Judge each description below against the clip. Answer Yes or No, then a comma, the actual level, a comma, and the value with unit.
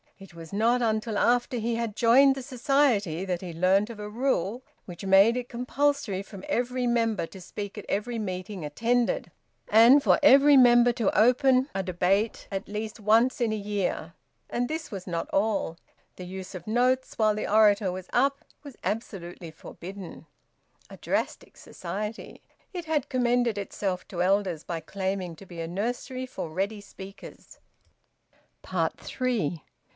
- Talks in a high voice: Yes, high, 215 Hz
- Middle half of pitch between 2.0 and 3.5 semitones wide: No, average, 4.4 semitones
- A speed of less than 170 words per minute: Yes, average, 160 wpm